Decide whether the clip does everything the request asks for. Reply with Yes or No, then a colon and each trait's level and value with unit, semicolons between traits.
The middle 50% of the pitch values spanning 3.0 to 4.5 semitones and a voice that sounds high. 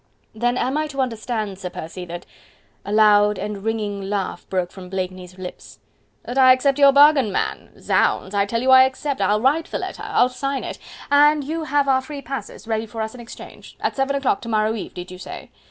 No: average, 5.2 semitones; high, 230 Hz